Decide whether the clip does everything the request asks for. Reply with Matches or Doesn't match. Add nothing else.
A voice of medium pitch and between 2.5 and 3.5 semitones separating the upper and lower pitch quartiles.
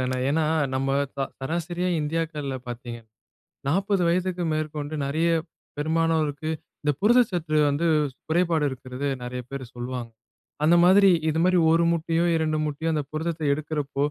Matches